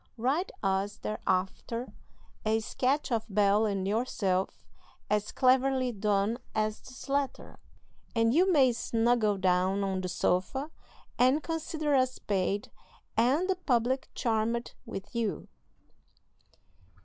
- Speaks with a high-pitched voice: Yes, high, 230 Hz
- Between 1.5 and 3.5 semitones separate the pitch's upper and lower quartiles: No, average, 4.6 semitones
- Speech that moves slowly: Yes, slow, 115 wpm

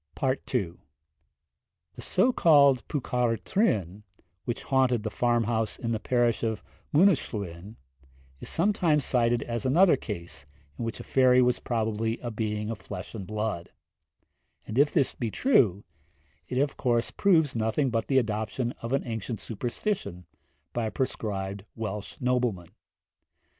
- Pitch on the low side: Yes, low, 115 Hz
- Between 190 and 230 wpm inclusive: No, average, 140 wpm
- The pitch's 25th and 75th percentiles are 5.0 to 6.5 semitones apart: No, average, 3.6 semitones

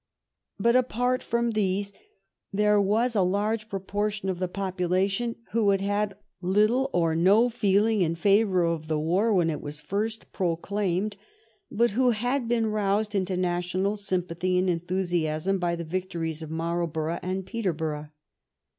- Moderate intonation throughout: Yes, average, 3.4 semitones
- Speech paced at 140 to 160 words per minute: Yes, average, 150 wpm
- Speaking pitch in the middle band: No, high, 195 Hz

